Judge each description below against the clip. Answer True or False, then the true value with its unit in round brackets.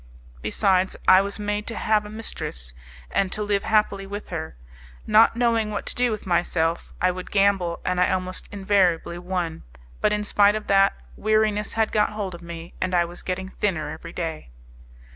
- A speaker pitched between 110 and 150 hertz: False (195 Hz)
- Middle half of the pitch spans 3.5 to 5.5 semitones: False (3.1 semitones)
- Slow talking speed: False (185 wpm)